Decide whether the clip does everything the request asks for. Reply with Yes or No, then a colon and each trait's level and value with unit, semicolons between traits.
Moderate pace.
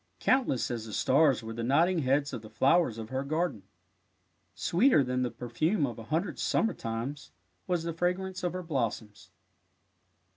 Yes: average, 175 wpm